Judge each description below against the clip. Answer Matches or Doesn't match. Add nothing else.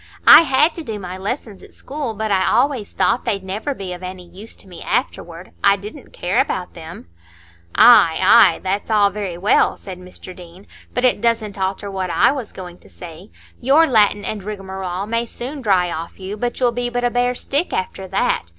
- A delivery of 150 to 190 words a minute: Doesn't match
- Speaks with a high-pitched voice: Matches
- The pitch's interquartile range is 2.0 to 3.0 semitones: Doesn't match